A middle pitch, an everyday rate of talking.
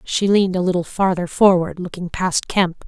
Yes: medium, 180 Hz; average, 190 wpm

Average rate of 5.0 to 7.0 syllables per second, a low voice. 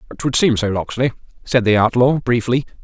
Yes: 5.5 syllables/s; low, 120 Hz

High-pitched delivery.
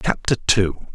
No: very low, 90 Hz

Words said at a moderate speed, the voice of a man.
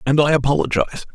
Yes: average, 155 wpm; male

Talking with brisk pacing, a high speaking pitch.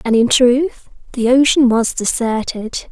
No: average, 145 wpm; high, 245 Hz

